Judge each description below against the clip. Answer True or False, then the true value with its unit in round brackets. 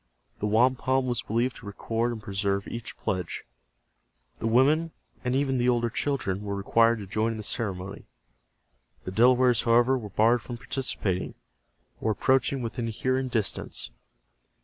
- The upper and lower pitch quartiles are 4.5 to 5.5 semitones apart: False (3.4 semitones)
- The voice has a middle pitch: False (115 Hz)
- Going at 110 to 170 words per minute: True (150 wpm)